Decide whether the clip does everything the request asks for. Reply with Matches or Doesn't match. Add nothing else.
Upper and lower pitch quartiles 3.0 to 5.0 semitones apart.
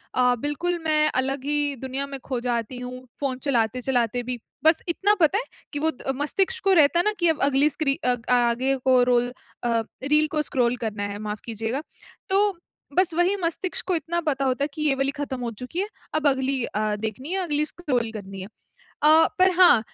Matches